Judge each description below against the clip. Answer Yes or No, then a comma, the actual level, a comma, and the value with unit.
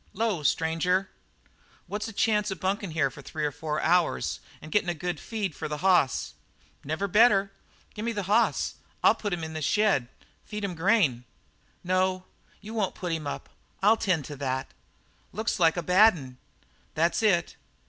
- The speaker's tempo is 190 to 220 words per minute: No, average, 180 wpm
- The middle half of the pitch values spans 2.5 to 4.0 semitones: No, average, 4.7 semitones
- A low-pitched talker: No, medium, 180 Hz